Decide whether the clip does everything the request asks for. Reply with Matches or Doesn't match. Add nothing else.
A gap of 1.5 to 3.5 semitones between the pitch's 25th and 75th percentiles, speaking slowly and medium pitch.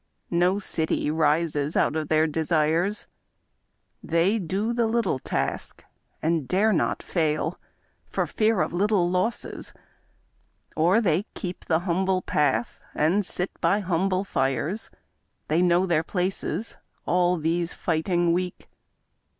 Matches